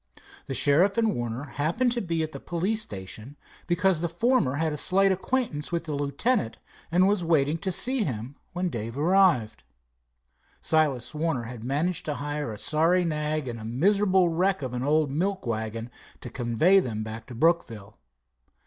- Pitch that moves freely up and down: Yes, wide, 6.7 semitones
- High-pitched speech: No, medium, 155 Hz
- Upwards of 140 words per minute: Yes, average, 175 wpm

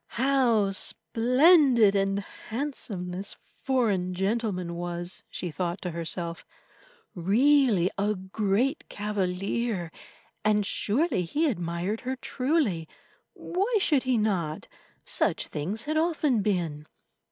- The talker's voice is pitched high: Yes, high, 205 Hz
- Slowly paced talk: Yes, slow, 105 wpm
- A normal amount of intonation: No, wide, 6.3 semitones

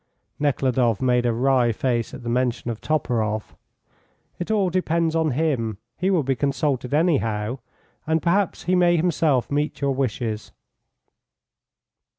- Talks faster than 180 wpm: No, average, 140 wpm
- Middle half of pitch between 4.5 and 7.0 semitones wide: Yes, average, 5.2 semitones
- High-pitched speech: No, low, 135 Hz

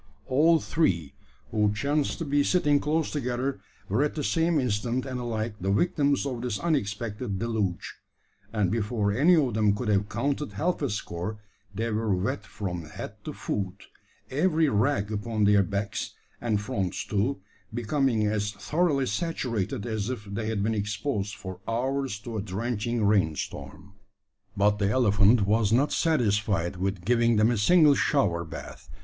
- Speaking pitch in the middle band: No, low, 110 Hz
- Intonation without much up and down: No, average, 5.0 semitones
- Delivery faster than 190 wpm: No, average, 160 wpm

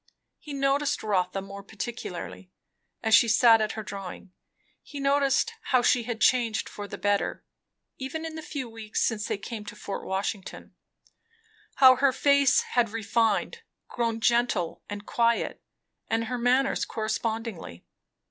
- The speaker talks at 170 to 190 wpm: No, average, 145 wpm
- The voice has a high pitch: Yes, high, 230 Hz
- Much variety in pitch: No, average, 4.1 semitones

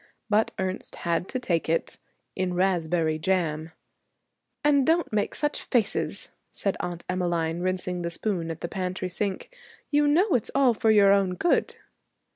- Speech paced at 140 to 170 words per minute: Yes, average, 155 wpm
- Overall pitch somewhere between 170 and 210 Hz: Yes, medium, 185 Hz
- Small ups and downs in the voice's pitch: No, average, 4.3 semitones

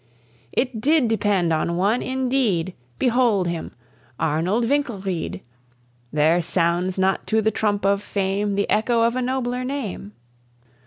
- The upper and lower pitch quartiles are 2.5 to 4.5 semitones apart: No, average, 5.2 semitones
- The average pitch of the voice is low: No, high, 205 Hz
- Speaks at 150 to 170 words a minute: No, slow, 135 wpm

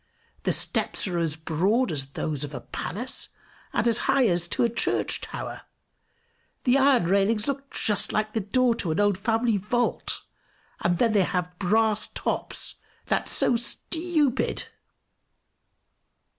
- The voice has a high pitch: Yes, high, 210 Hz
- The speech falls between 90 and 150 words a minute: Yes, average, 145 wpm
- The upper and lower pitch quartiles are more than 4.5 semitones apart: Yes, wide, 5.4 semitones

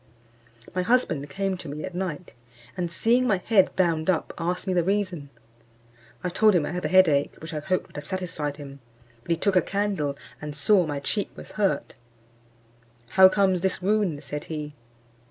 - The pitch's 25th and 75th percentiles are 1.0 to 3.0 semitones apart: No, average, 4.2 semitones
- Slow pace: No, average, 190 wpm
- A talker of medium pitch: Yes, medium, 180 Hz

